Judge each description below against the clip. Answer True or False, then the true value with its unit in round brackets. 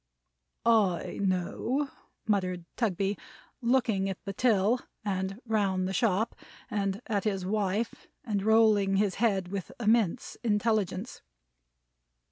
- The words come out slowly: True (115 wpm)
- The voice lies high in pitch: True (205 Hz)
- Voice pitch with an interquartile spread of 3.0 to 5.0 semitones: False (2.6 semitones)